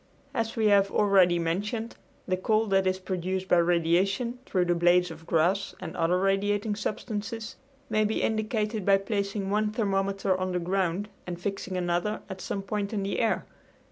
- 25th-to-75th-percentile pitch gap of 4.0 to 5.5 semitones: No, average, 2.7 semitones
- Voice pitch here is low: No, high, 195 Hz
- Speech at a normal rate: Yes, average, 170 wpm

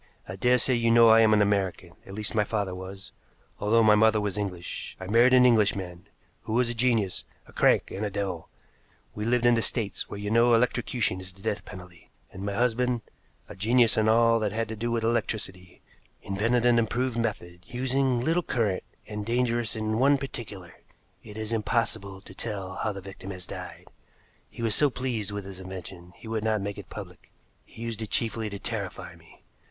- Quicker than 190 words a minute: Yes, average, 200 wpm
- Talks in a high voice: No, low, 110 Hz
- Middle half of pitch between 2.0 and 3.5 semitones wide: Yes, average, 3.1 semitones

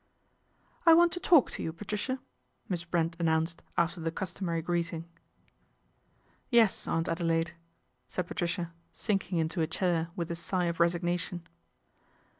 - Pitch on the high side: No, medium, 170 Hz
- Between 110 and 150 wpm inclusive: Yes, average, 145 wpm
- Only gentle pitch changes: Yes, narrow, 2.1 semitones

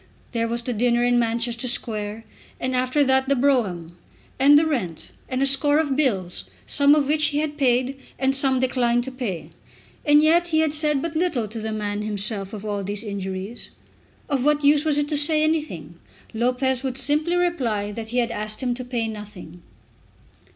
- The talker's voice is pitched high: Yes, very high, 250 Hz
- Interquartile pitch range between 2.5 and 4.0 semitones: No, average, 5.1 semitones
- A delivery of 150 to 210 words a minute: Yes, average, 195 wpm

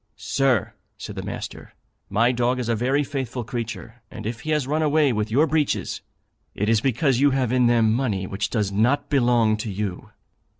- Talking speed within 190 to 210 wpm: Yes, average, 195 wpm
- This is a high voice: No, low, 120 Hz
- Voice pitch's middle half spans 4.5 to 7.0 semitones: No, average, 3.7 semitones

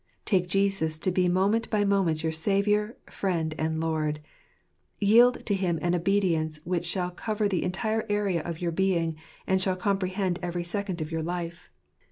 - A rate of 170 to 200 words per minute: Yes, average, 175 wpm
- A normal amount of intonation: Yes, average, 3.1 semitones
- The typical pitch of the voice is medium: Yes, medium, 180 Hz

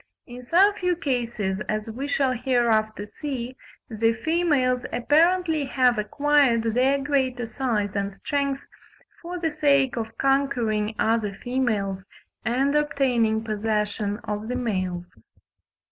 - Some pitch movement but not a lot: Yes, average, 4.4 semitones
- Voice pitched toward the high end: Yes, high, 245 Hz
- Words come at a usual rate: No, slow, 120 wpm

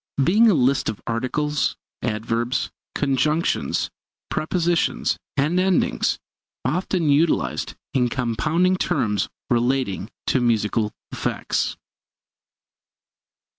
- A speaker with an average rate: No, slow, 85 wpm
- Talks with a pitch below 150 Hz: Yes, low, 135 Hz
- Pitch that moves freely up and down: Yes, wide, 6.0 semitones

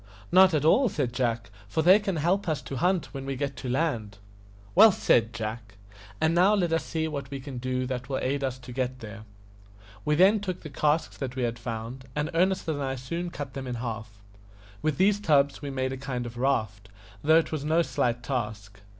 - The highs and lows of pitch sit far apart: No, average, 4.8 semitones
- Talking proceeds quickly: Yes, fast, 220 wpm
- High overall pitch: No, low, 135 Hz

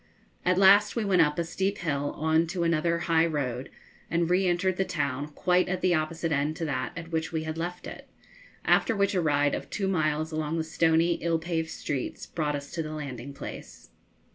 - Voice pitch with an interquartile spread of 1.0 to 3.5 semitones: Yes, average, 2.8 semitones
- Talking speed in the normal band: No, fast, 210 wpm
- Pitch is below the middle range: No, medium, 165 Hz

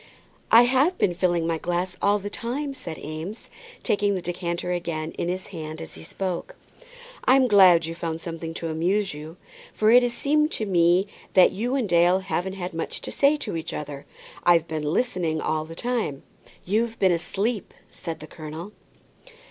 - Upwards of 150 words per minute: Yes, average, 180 wpm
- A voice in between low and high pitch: Yes, medium, 180 Hz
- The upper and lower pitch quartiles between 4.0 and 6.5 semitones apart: Yes, average, 4.3 semitones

